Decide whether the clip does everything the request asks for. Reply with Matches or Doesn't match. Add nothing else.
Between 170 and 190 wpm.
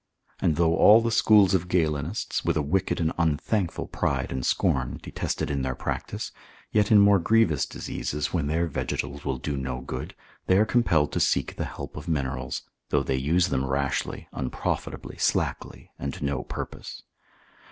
Matches